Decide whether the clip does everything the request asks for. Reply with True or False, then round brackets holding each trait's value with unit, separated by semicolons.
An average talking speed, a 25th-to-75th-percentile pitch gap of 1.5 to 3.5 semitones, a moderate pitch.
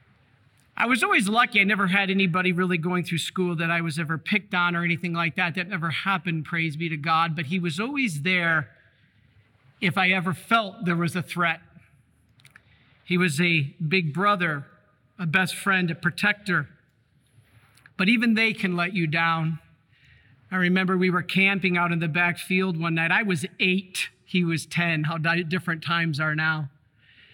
True (180 wpm; 3.1 semitones; 170 Hz)